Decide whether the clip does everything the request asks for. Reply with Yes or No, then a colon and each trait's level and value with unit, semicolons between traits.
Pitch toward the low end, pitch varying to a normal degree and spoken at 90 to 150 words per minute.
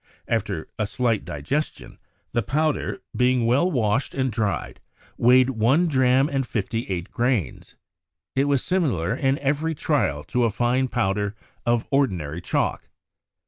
Yes: low, 125 Hz; average, 4.4 semitones; average, 140 wpm